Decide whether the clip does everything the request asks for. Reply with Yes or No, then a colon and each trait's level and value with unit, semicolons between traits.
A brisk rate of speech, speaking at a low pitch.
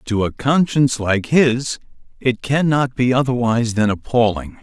No: average, 145 wpm; low, 125 Hz